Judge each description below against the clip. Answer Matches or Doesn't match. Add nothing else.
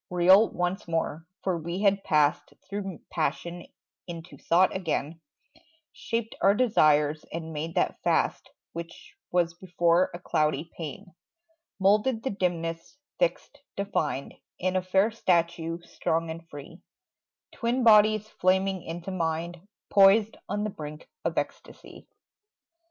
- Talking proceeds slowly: Matches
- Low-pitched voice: Doesn't match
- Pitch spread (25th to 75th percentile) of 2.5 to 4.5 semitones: Matches